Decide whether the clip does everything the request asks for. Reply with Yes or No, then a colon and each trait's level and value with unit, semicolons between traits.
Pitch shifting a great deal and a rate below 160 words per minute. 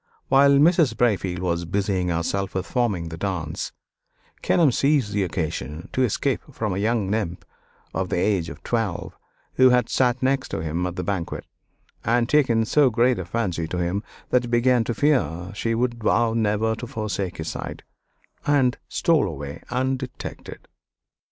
No: wide, 5.7 semitones; average, 165 wpm